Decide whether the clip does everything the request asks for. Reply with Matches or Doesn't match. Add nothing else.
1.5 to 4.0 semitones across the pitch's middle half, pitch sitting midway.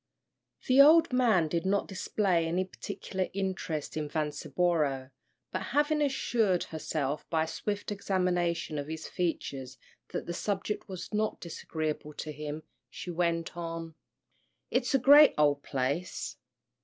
Doesn't match